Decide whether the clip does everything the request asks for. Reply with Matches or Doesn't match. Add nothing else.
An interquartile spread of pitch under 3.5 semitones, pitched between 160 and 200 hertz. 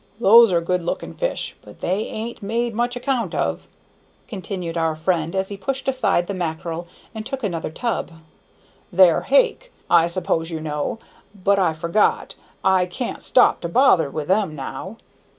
Doesn't match